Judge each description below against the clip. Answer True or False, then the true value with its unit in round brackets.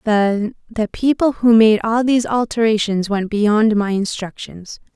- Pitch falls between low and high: False (215 Hz)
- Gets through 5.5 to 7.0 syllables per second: False (4.2 syllables/s)